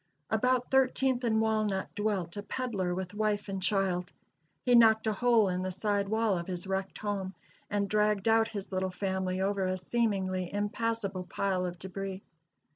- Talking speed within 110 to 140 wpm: No, average, 170 wpm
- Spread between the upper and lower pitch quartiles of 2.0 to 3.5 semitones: Yes, average, 2.8 semitones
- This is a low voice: No, high, 200 Hz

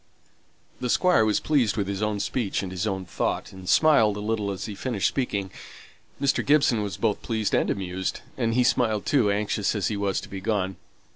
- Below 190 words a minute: No, fast, 205 wpm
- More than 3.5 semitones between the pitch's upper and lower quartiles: No, average, 2.9 semitones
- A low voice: Yes, low, 105 Hz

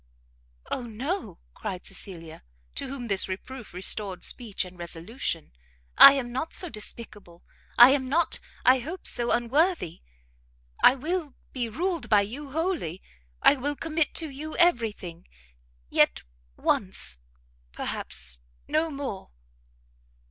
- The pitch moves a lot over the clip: Yes, wide, 7.6 semitones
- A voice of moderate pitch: No, high, 245 Hz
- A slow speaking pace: Yes, slow, 125 wpm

